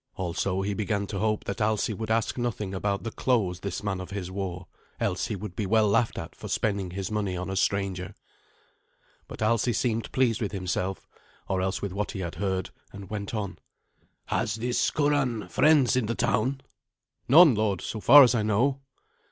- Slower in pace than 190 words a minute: No, average, 195 wpm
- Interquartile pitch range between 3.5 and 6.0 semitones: No, average, 3.1 semitones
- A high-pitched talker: No, low, 105 Hz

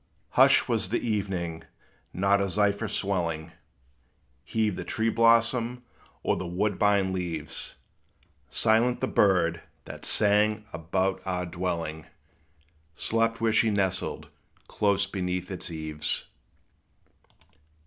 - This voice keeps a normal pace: No, slow, 105 wpm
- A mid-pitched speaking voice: No, very low, 95 Hz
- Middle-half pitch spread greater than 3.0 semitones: Yes, average, 3.5 semitones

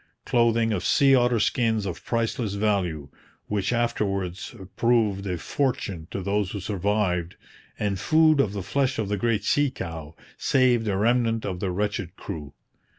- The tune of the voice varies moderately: Yes, average, 3.9 semitones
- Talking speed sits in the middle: Yes, average, 155 wpm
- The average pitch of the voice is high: No, low, 105 Hz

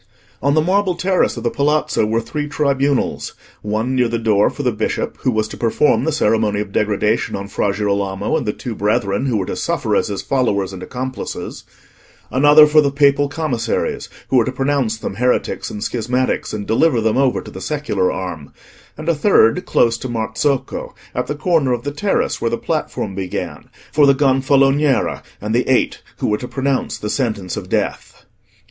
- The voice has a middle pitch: No, low, 125 Hz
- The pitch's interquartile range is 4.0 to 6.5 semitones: Yes, average, 4.9 semitones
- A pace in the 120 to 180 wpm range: No, average, 190 wpm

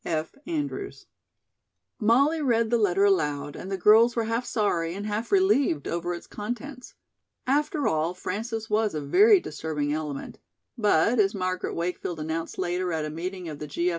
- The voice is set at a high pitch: Yes, high, 195 Hz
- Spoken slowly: No, average, 165 wpm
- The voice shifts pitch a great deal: Yes, wide, 6.2 semitones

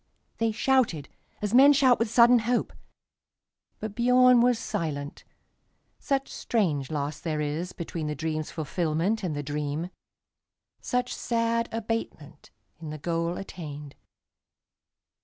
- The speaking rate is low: Yes, slow, 110 wpm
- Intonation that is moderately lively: No, wide, 7.5 semitones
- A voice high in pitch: No, medium, 180 Hz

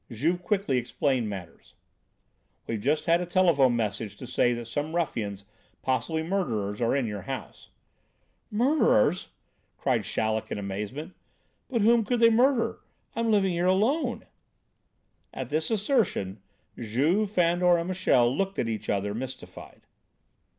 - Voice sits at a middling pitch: Yes, medium, 155 Hz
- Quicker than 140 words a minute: No, slow, 135 wpm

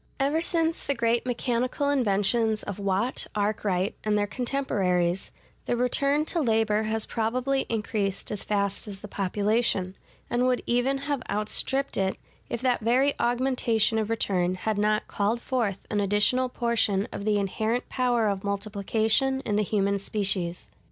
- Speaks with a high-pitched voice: Yes, high, 220 Hz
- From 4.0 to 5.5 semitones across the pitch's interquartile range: No, average, 3.6 semitones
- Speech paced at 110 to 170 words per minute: Yes, average, 150 wpm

